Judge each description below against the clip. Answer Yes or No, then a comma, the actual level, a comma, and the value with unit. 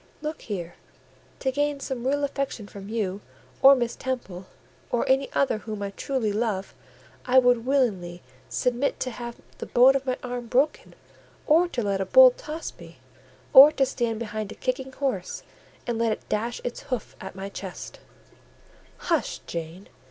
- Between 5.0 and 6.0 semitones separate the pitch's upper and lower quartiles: No, average, 4.6 semitones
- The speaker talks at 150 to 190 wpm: Yes, average, 165 wpm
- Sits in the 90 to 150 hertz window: No, high, 240 Hz